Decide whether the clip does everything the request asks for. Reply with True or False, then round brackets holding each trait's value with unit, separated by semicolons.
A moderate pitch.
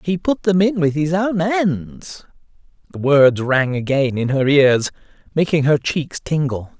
True (155 Hz)